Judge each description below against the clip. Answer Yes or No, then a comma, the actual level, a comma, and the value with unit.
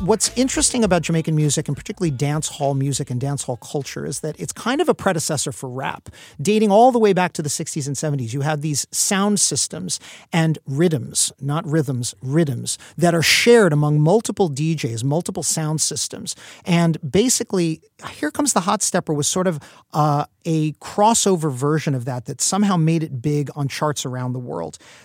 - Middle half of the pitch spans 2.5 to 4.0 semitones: No, average, 4.5 semitones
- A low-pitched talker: No, medium, 155 Hz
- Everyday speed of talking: Yes, average, 185 wpm